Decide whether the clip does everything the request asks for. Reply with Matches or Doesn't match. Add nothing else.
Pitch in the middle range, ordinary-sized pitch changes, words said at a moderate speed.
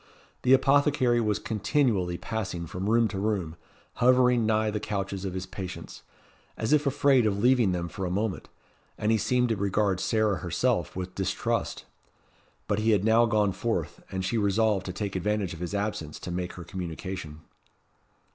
Doesn't match